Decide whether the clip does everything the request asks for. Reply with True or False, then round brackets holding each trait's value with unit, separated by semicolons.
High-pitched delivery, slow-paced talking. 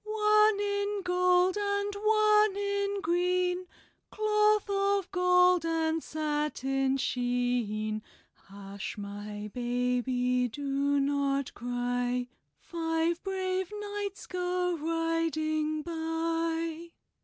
True (330 Hz; 85 wpm)